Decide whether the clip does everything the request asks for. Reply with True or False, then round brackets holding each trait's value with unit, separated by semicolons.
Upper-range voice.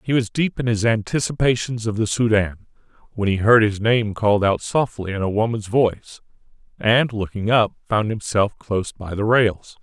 False (110 Hz)